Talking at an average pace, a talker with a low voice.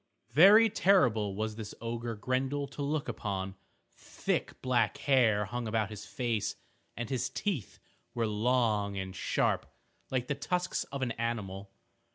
Yes: average, 145 wpm; low, 115 Hz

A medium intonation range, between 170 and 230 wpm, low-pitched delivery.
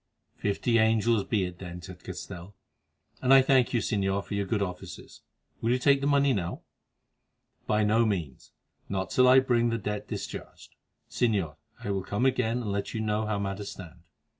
Yes: average, 3.6 semitones; average, 185 wpm; low, 105 Hz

